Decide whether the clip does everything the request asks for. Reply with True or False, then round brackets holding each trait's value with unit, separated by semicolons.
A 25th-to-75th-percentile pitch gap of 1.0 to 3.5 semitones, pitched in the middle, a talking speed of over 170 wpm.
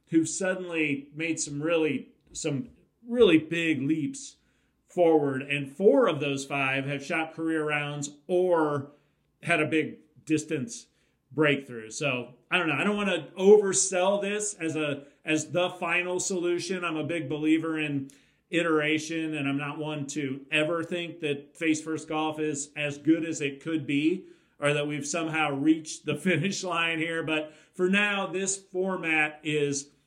False (2.9 semitones; 160 Hz; 160 wpm)